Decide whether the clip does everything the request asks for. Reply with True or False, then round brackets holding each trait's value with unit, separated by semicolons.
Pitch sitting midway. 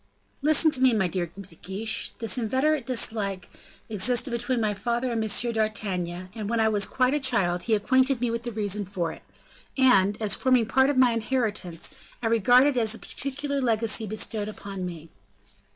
False (225 Hz)